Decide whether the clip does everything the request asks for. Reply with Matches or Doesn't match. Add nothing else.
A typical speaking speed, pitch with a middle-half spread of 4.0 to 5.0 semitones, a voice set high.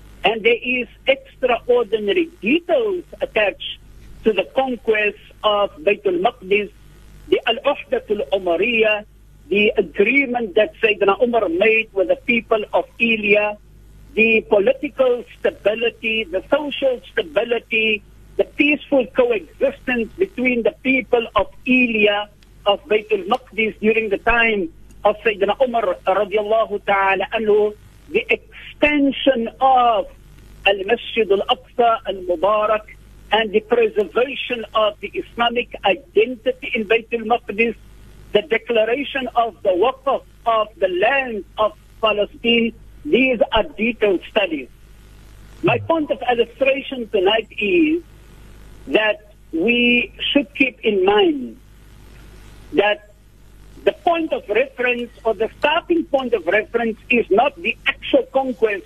Doesn't match